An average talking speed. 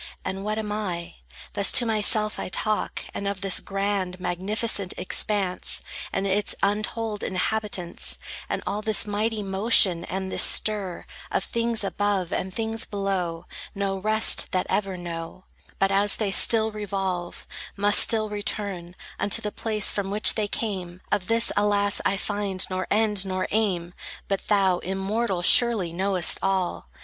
Yes: average, 150 wpm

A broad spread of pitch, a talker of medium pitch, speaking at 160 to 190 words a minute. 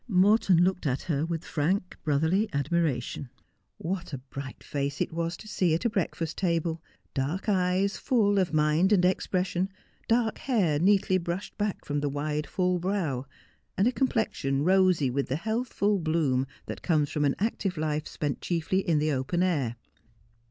No: average, 4.4 semitones; medium, 170 Hz; average, 175 wpm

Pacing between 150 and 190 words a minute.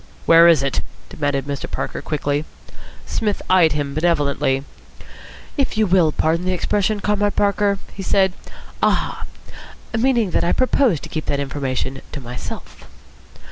No: average, 140 wpm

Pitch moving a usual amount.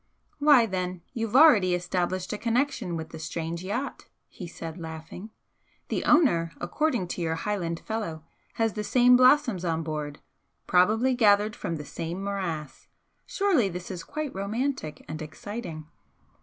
No: wide, 5.9 semitones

